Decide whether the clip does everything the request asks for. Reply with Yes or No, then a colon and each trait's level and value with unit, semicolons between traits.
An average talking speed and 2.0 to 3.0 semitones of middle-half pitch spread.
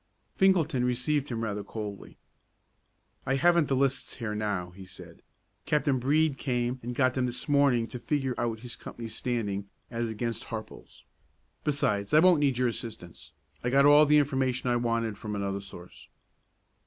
No: average, 165 wpm; average, 4.0 semitones